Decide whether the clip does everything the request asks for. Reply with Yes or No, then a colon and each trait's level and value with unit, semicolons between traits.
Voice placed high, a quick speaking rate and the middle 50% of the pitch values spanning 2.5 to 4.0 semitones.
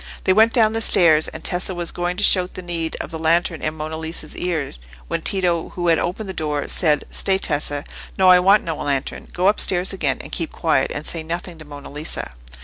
No: medium, 170 Hz; fast, 220 wpm; average, 2.9 semitones